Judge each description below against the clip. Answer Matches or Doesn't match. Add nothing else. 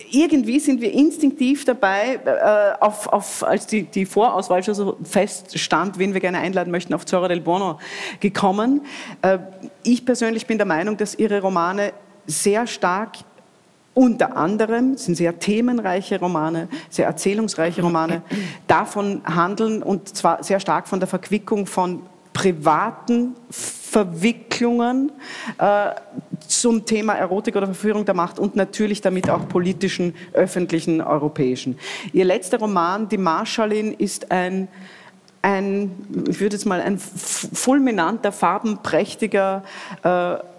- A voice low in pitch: Doesn't match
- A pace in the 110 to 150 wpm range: Matches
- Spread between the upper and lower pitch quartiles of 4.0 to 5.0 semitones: Doesn't match